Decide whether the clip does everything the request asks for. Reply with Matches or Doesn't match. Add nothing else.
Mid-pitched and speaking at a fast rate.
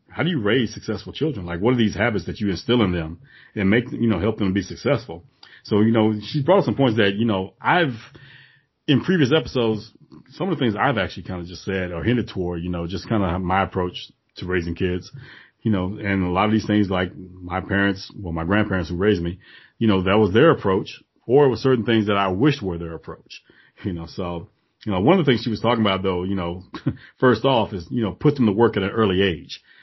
Doesn't match